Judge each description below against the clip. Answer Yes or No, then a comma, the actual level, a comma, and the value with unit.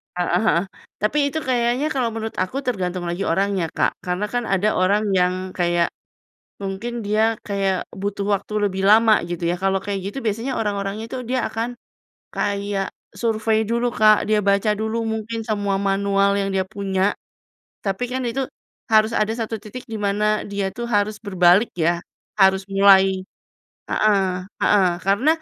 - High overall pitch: Yes, high, 205 Hz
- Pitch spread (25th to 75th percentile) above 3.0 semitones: No, narrow, 2.4 semitones